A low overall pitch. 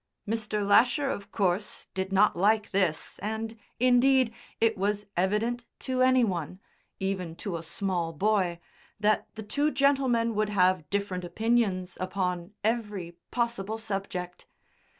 No: high, 205 Hz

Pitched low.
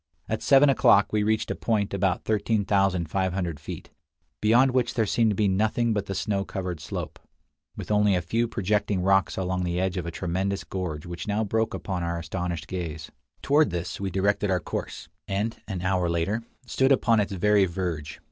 Yes: very low, 95 Hz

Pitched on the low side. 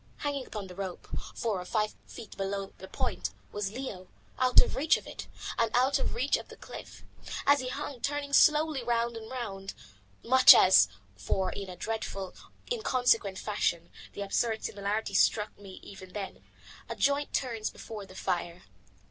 No: high, 220 Hz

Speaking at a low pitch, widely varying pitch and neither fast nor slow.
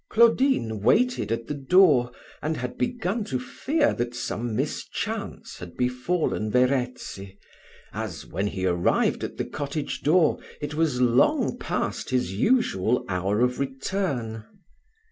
No: low, 125 Hz; wide, 6.5 semitones; slow, 130 wpm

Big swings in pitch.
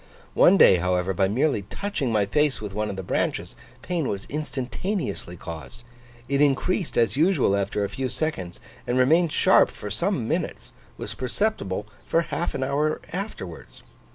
Yes: wide, 8.2 semitones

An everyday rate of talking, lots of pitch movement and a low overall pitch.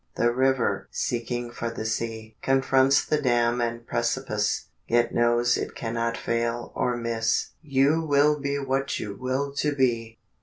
No: average, 150 wpm; narrow, 2.4 semitones; low, 120 Hz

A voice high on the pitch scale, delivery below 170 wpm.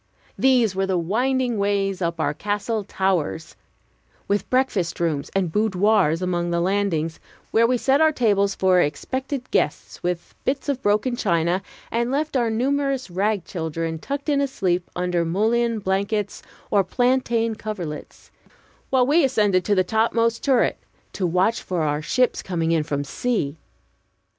Yes: high, 200 Hz; average, 150 wpm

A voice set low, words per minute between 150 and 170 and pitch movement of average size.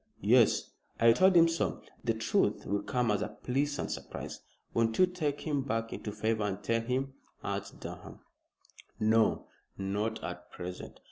Yes: low, 115 Hz; average, 155 wpm; average, 4.6 semitones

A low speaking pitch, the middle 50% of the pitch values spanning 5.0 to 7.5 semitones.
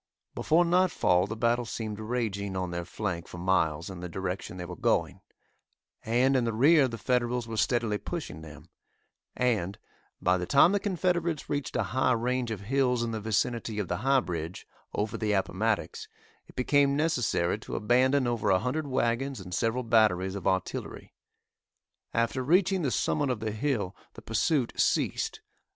Yes: low, 115 Hz; wide, 5.4 semitones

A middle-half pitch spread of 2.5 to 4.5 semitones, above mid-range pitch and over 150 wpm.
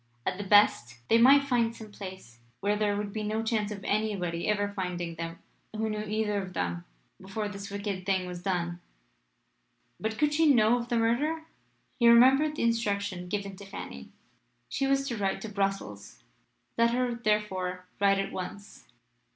Yes: average, 3.4 semitones; high, 205 Hz; average, 175 wpm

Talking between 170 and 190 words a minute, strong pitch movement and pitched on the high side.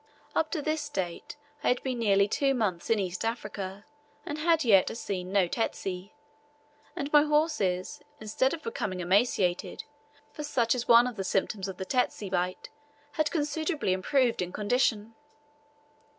No: average, 160 wpm; wide, 6.8 semitones; high, 225 Hz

